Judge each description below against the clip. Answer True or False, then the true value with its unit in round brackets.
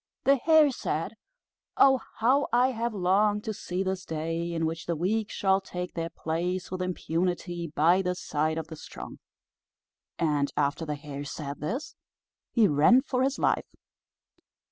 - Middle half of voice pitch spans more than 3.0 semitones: True (5.4 semitones)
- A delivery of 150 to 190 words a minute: True (160 wpm)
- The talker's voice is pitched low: False (180 Hz)